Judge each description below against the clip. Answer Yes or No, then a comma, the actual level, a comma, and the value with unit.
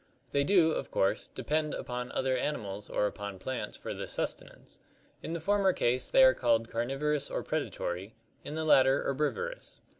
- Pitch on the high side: No, low, 135 Hz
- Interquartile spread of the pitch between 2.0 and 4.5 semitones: No, average, 5.3 semitones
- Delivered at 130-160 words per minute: No, average, 170 wpm